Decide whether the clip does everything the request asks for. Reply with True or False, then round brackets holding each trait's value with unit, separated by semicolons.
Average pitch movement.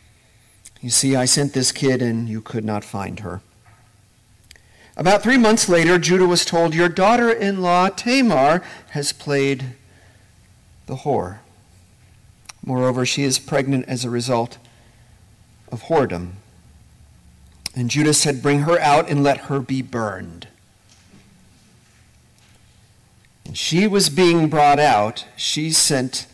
False (6.0 semitones)